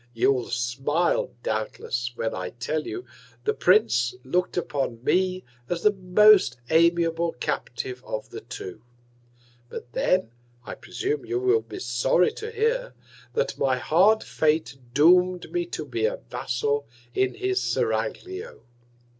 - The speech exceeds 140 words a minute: No, slow, 135 wpm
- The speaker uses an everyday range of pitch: No, wide, 7.4 semitones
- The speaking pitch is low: No, medium, 155 Hz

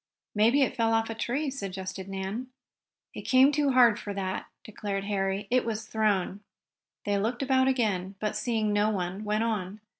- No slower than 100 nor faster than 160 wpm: No, average, 175 wpm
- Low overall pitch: No, high, 215 Hz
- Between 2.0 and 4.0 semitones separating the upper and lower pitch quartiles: Yes, average, 3.5 semitones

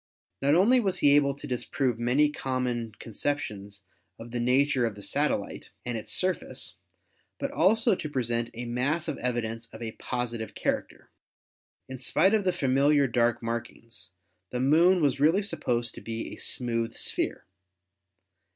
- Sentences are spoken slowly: No, average, 155 wpm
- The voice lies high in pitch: No, low, 125 Hz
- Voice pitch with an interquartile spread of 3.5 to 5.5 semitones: Yes, average, 4.0 semitones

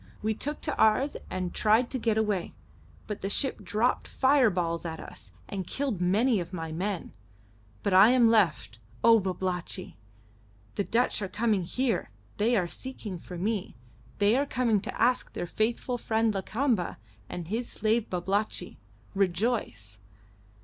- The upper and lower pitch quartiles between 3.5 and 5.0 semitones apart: Yes, average, 4.5 semitones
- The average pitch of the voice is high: Yes, high, 210 Hz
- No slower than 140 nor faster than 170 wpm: Yes, average, 150 wpm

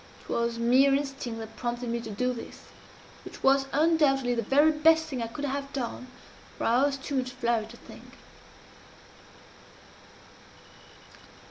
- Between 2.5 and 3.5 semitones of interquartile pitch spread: Yes, average, 2.9 semitones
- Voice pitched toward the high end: Yes, very high, 260 Hz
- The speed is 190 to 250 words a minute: No, average, 150 wpm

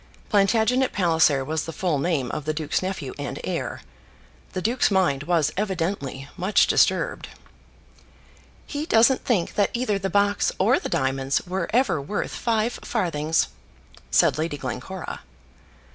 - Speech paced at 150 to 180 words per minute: No, average, 140 wpm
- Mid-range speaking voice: Yes, medium, 180 Hz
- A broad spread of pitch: Yes, wide, 5.7 semitones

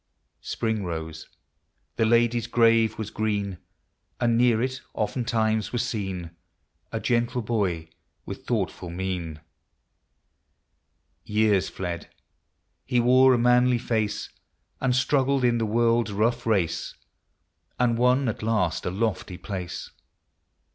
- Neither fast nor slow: No, slow, 120 wpm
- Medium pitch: No, low, 110 Hz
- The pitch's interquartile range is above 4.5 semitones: No, average, 3.7 semitones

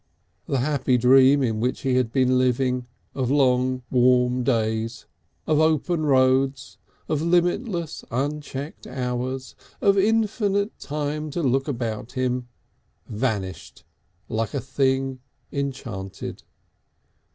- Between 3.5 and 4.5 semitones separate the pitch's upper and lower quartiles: No, average, 2.9 semitones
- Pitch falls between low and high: No, low, 130 Hz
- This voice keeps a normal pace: No, slow, 110 wpm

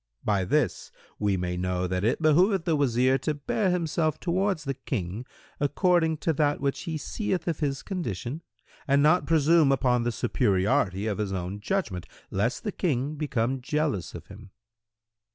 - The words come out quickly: No, average, 165 wpm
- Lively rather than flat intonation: Yes, wide, 7.3 semitones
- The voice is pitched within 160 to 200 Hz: No, medium, 140 Hz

